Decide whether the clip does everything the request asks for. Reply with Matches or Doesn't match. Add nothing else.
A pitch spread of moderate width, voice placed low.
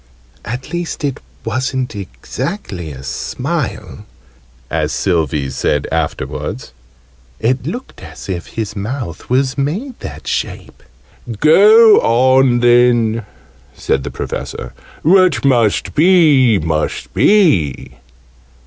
Doesn't match